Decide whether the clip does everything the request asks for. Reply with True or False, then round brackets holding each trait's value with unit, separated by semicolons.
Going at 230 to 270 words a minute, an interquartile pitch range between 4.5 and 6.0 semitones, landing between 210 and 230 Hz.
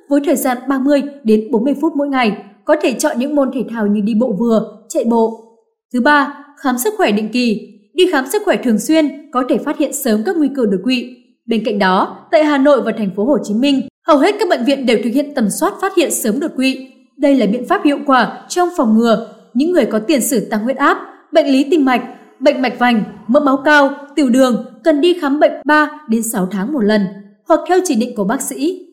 False (245 wpm; 4.9 semitones; 265 Hz)